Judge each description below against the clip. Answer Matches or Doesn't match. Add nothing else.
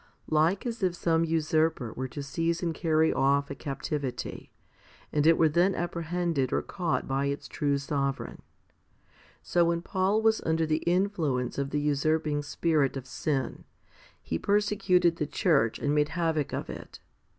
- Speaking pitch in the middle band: Matches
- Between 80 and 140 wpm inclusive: Doesn't match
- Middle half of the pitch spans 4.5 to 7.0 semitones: Doesn't match